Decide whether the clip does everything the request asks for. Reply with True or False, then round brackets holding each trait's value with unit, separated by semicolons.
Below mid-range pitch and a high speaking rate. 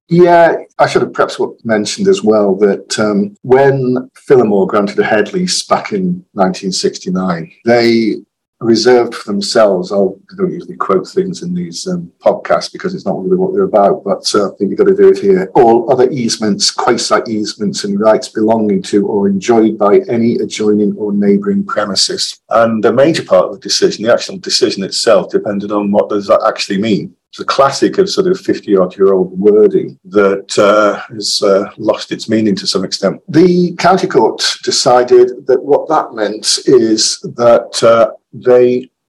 False (125 Hz; 180 wpm)